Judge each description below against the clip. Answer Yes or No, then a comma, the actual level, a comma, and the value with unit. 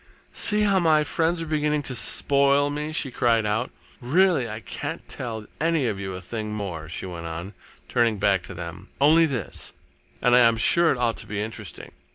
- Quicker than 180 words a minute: Yes, average, 200 wpm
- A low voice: Yes, low, 120 Hz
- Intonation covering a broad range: Yes, wide, 6.5 semitones